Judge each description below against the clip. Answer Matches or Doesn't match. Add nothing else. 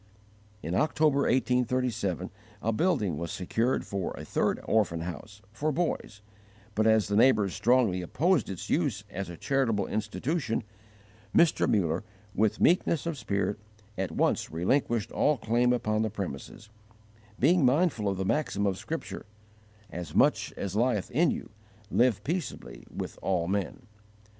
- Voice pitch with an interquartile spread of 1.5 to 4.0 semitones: Doesn't match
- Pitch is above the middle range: Doesn't match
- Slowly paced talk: Doesn't match